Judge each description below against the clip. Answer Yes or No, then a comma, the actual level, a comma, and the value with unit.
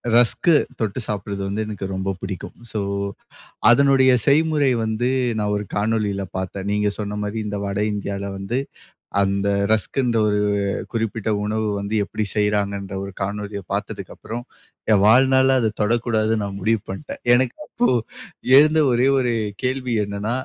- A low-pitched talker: Yes, low, 105 Hz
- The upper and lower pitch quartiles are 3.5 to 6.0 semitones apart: No, average, 3.1 semitones